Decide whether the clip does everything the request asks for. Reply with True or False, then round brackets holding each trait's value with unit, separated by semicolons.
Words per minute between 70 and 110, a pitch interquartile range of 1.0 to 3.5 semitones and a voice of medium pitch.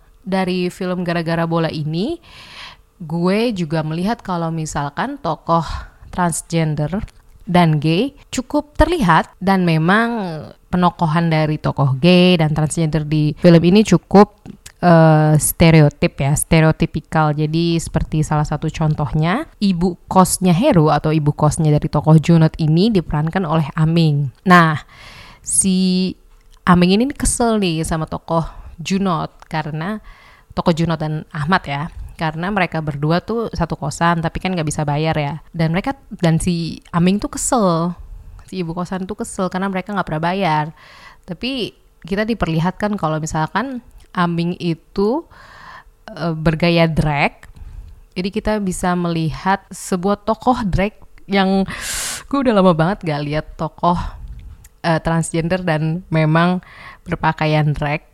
False (130 wpm; 3.1 semitones; 170 Hz)